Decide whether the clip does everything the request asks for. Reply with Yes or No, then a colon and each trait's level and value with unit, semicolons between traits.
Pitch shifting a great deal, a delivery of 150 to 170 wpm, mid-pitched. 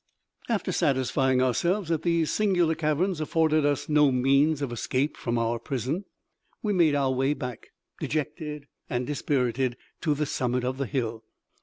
No: average, 3.6 semitones; average, 155 wpm; medium, 145 Hz